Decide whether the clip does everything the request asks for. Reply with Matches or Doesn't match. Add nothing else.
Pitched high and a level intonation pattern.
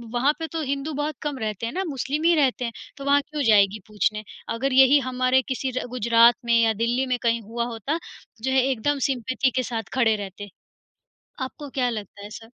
Doesn't match